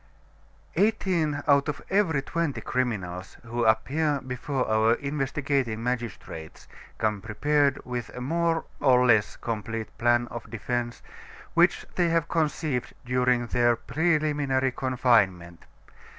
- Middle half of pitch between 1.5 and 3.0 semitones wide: No, average, 4.2 semitones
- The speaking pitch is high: No, low, 125 Hz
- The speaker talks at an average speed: No, slow, 115 wpm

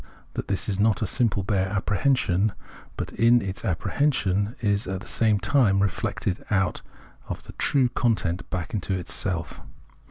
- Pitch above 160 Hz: No, low, 100 Hz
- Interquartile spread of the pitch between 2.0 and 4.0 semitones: Yes, average, 3.1 semitones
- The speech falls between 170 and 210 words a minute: No, average, 155 wpm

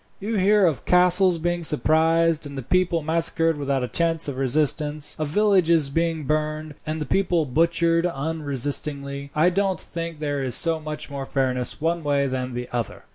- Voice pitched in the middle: Yes, medium, 155 Hz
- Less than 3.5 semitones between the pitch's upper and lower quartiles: Yes, average, 3.1 semitones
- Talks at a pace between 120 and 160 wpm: No, average, 175 wpm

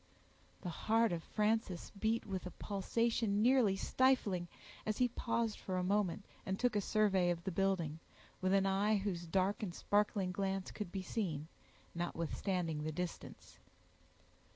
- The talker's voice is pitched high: Yes, high, 195 Hz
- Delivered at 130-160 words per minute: Yes, average, 150 wpm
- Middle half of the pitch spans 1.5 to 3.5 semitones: Yes, average, 3.1 semitones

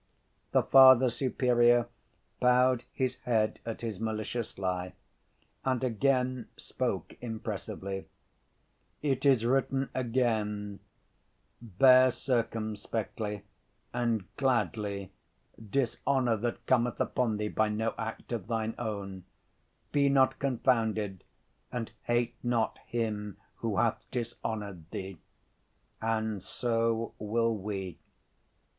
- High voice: No, low, 115 Hz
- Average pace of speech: No, slow, 100 wpm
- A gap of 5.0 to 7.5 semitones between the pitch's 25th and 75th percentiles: No, average, 2.9 semitones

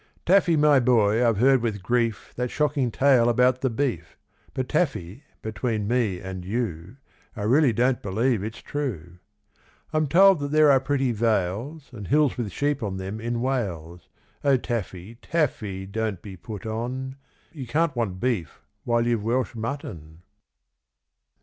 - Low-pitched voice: Yes, low, 120 Hz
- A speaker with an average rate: Yes, average, 155 wpm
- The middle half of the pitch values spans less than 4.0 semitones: No, average, 4.7 semitones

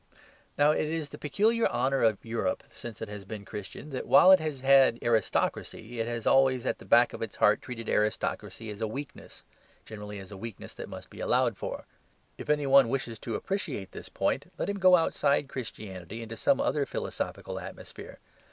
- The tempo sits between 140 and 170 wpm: No, average, 195 wpm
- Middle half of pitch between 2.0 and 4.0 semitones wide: No, average, 4.7 semitones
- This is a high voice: No, low, 120 Hz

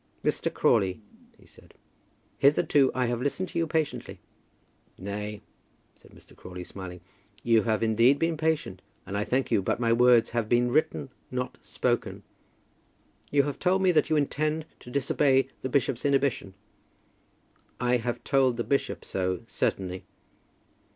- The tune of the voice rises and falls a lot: No, average, 4.9 semitones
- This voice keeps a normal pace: Yes, average, 150 wpm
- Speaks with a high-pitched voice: No, low, 125 Hz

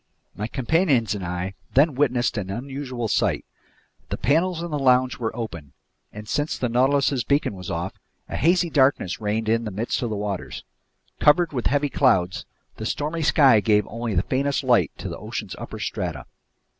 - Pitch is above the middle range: No, low, 125 Hz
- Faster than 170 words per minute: Yes, average, 180 wpm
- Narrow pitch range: No, average, 5.1 semitones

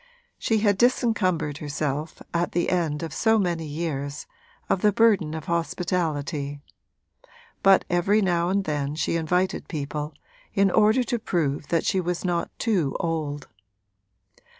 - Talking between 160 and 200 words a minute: No, average, 140 wpm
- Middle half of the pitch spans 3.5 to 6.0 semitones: Yes, average, 4.4 semitones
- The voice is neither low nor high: Yes, medium, 170 Hz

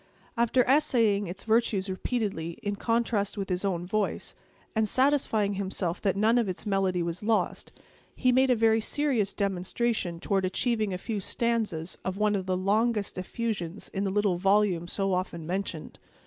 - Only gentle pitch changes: No, average, 3.5 semitones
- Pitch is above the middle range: Yes, high, 200 Hz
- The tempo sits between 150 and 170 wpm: Yes, average, 165 wpm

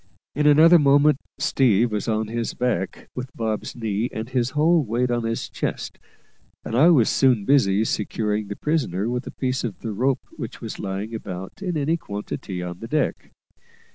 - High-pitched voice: No, low, 120 Hz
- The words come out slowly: No, average, 180 wpm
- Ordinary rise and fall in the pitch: Yes, average, 4.5 semitones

